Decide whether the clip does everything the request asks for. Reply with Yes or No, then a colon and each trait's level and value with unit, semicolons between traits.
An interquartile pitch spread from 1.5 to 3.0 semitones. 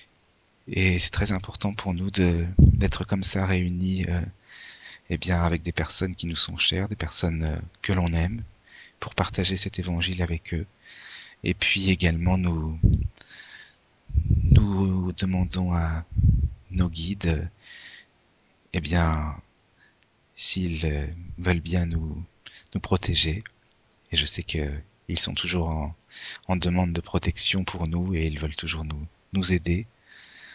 Yes: narrow, 2.4 semitones